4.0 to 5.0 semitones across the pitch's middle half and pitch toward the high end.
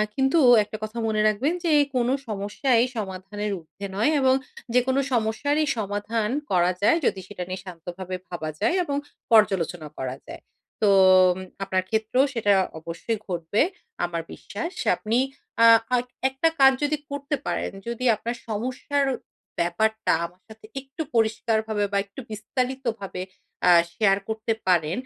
Yes: average, 4.6 semitones; high, 220 Hz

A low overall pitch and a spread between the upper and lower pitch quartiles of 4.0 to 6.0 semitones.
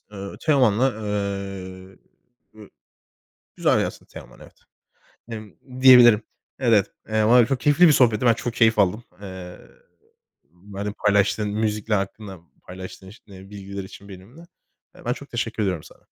No: low, 105 Hz; average, 3.0 semitones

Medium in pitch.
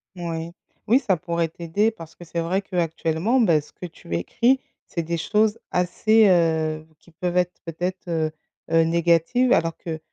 Yes: medium, 170 Hz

